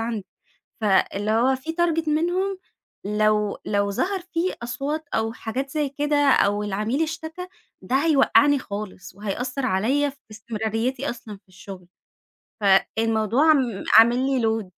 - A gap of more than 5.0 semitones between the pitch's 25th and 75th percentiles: Yes, wide, 5.5 semitones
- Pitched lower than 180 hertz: No, high, 240 Hz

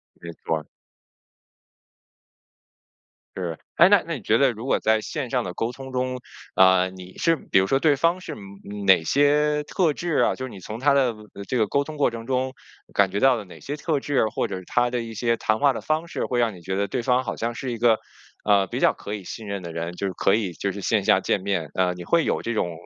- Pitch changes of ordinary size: No, wide, 5.7 semitones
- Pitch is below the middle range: Yes, low, 115 Hz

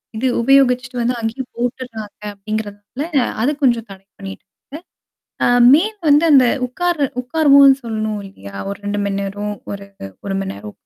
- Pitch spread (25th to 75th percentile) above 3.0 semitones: Yes, average, 4.6 semitones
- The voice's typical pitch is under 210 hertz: No, high, 225 Hz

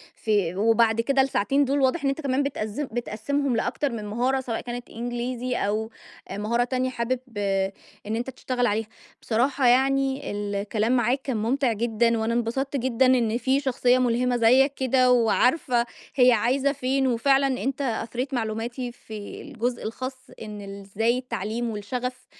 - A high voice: Yes, high, 245 Hz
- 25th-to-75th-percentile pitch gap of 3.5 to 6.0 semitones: No, average, 2.8 semitones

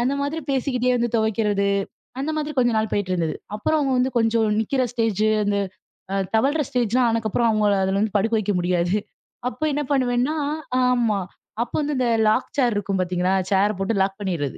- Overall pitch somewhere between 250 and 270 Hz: No, high, 225 Hz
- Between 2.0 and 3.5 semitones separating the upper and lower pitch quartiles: No, average, 3.9 semitones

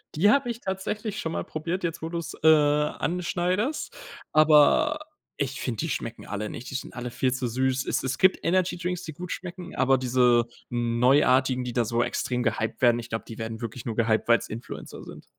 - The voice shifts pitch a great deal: Yes, wide, 6.5 semitones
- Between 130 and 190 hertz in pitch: Yes, low, 135 Hz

